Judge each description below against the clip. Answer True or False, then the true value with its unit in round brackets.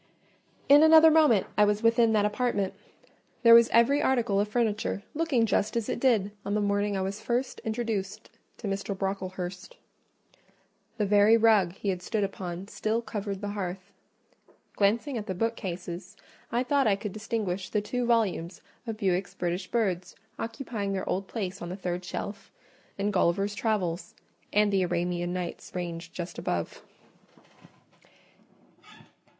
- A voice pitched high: True (205 Hz)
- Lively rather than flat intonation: False (3.4 semitones)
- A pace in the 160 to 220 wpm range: False (150 wpm)